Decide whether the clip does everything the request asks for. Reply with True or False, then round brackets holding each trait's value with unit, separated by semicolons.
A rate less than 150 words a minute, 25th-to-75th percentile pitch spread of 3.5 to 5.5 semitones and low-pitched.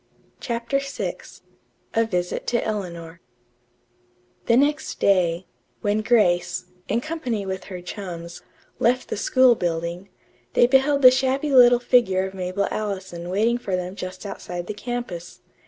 False (140 wpm; 5.2 semitones; 205 Hz)